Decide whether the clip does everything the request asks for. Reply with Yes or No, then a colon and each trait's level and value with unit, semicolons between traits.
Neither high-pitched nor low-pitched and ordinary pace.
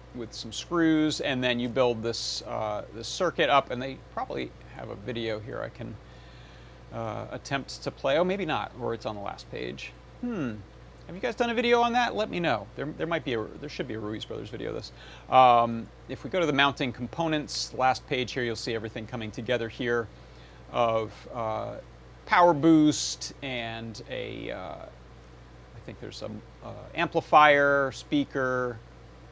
No: low, 125 Hz; average, 190 wpm